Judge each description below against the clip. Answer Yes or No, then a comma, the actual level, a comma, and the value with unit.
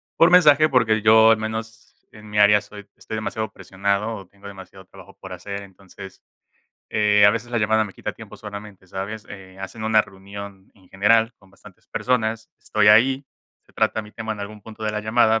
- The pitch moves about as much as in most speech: No, narrow, 2.0 semitones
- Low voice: Yes, low, 105 Hz